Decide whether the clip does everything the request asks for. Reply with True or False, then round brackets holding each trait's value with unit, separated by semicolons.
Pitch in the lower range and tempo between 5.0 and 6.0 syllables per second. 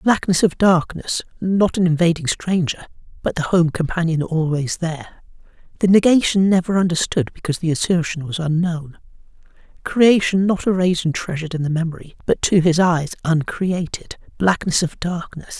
False (170 Hz; 5.2 syllables/s)